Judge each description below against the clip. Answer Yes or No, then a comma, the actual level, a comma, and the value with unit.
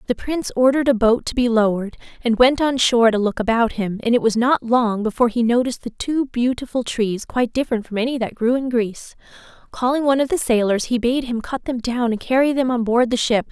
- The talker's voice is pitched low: No, high, 240 Hz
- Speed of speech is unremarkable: No, fast, 240 wpm